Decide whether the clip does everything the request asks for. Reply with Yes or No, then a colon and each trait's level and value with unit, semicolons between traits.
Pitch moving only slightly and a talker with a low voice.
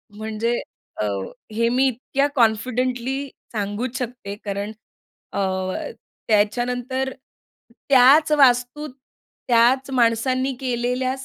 No: narrow, 2.3 semitones; high, 245 Hz